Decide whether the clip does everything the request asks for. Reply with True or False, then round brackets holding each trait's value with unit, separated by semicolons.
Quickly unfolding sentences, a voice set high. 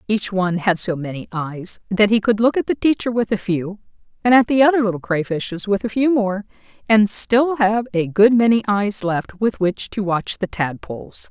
True (210 wpm; 200 Hz)